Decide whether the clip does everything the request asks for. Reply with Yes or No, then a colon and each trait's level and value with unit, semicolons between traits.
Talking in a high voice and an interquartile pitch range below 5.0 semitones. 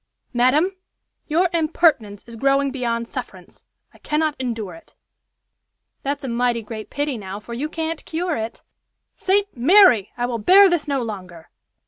No: very high, 260 Hz; wide, 5.6 semitones